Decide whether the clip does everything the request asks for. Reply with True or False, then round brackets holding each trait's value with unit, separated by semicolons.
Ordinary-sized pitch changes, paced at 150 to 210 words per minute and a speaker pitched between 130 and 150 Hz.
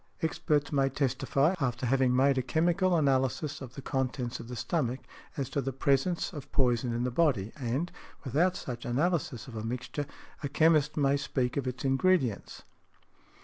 True (3.3 semitones; 170 wpm; 135 Hz)